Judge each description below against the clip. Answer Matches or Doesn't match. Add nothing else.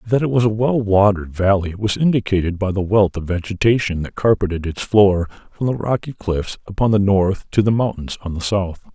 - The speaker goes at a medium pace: Doesn't match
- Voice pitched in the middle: Doesn't match